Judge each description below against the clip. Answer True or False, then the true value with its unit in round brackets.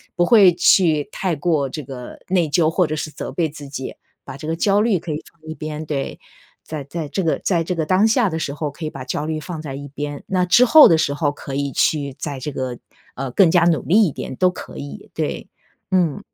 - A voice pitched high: False (155 Hz)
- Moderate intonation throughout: True (3.8 semitones)